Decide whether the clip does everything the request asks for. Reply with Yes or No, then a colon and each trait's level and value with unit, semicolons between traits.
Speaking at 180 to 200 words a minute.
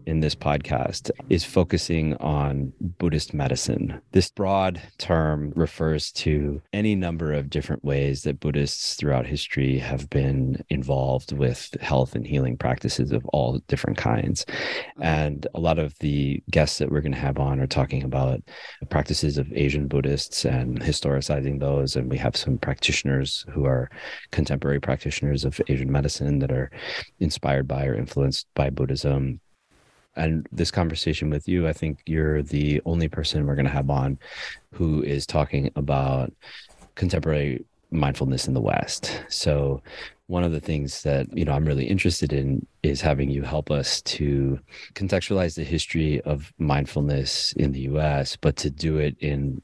No: average, 160 wpm